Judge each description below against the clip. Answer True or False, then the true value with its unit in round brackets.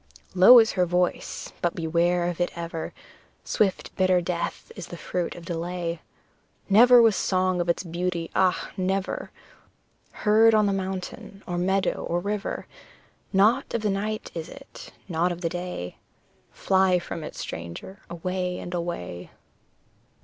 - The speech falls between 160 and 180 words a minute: False (150 wpm)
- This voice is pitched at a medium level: True (180 Hz)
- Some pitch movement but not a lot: False (2.1 semitones)